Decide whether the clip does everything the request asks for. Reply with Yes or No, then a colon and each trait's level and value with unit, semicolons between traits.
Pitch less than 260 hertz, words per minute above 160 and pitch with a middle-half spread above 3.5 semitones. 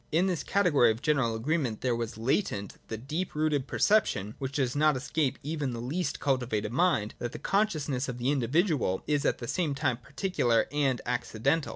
Yes: low, 135 Hz; average, 185 wpm; average, 4.6 semitones